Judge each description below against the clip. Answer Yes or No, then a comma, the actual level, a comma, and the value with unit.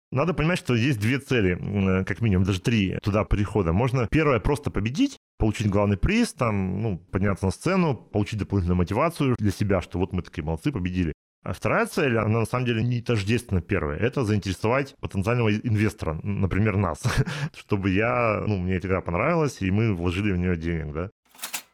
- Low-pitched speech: Yes, low, 105 Hz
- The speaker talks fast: Yes, fast, 180 wpm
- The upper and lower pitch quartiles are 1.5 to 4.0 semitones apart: No, average, 4.4 semitones